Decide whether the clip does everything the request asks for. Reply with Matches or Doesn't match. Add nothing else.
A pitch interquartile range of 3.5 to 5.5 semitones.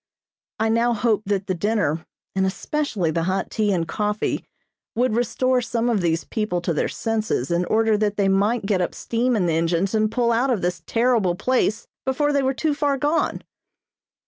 Matches